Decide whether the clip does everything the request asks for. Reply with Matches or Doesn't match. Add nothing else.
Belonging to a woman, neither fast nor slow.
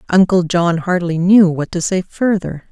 Matches